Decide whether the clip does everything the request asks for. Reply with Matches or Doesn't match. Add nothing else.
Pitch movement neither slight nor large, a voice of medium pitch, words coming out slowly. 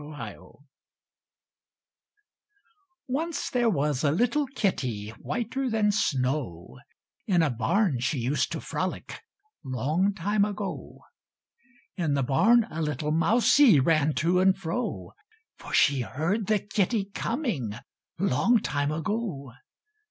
Doesn't match